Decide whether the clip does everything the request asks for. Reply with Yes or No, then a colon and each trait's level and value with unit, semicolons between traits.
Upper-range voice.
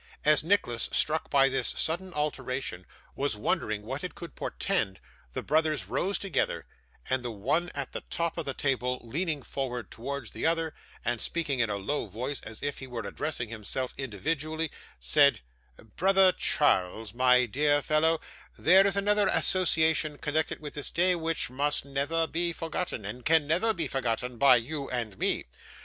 No: medium, 145 Hz